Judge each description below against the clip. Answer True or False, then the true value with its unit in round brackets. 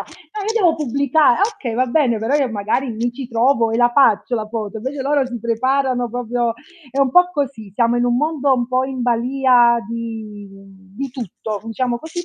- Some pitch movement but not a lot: True (3.1 semitones)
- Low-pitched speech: False (245 Hz)